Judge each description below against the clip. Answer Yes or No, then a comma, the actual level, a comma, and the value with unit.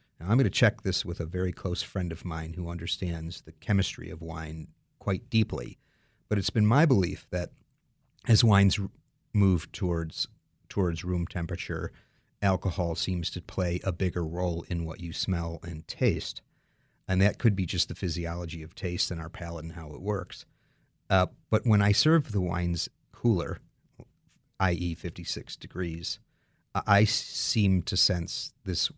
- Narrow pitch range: No, average, 3.7 semitones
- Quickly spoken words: No, average, 165 wpm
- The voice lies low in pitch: Yes, very low, 95 Hz